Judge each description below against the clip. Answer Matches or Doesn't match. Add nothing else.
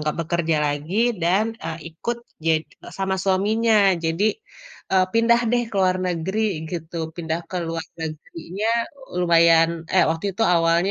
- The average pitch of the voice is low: Doesn't match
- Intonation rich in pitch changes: Doesn't match